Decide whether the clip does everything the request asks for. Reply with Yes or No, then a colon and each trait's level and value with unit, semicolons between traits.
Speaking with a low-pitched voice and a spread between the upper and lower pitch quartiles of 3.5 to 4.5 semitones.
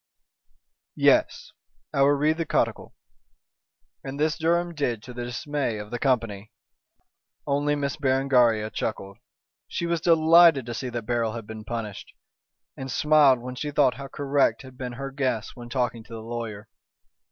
Yes: low, 130 Hz; average, 3.8 semitones